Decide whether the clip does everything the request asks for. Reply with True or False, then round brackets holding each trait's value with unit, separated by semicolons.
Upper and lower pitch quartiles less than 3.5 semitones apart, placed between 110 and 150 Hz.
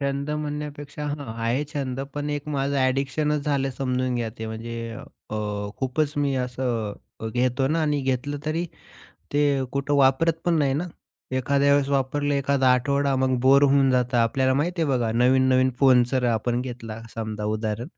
True (2.5 semitones; 135 Hz)